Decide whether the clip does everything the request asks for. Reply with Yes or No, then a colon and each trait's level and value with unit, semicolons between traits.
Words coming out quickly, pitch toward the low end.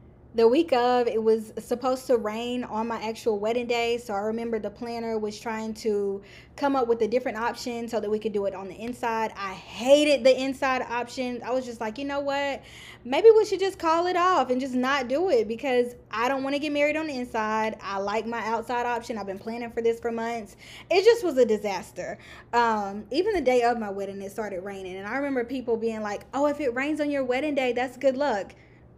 No: fast, 235 wpm; high, 240 Hz